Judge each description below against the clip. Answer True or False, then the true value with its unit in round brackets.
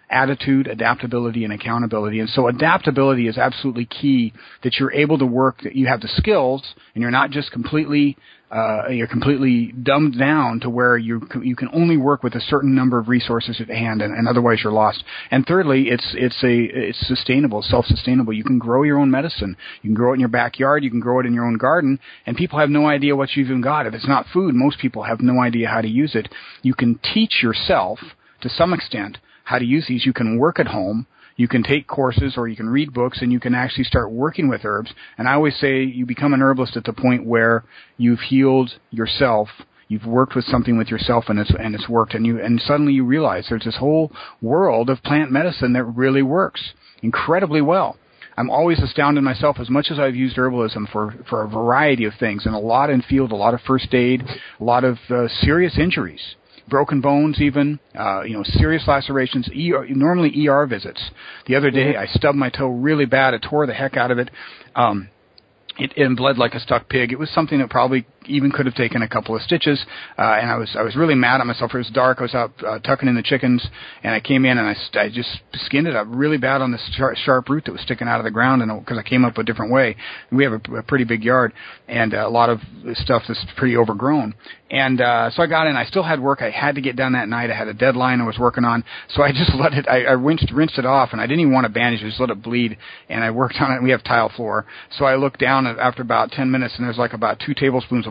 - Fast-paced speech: True (245 wpm)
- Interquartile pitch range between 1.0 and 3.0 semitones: True (2.7 semitones)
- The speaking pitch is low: True (125 Hz)